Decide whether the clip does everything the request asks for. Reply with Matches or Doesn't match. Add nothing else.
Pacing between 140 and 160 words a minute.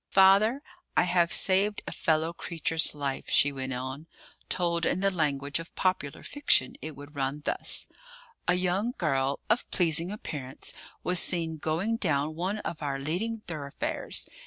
Matches